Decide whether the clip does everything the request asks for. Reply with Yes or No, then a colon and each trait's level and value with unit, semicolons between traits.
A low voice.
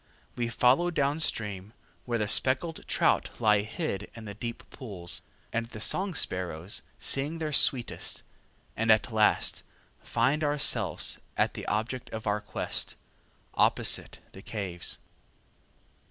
Yes: low, 115 Hz